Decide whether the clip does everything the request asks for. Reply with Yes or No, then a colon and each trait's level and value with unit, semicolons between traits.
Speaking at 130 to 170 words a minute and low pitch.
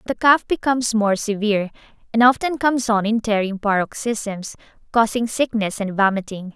No: average, 145 wpm; high, 220 Hz